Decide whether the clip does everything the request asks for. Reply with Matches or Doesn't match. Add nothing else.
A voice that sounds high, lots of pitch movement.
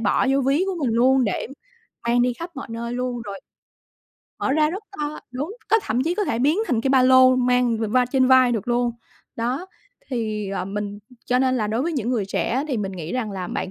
Doesn't match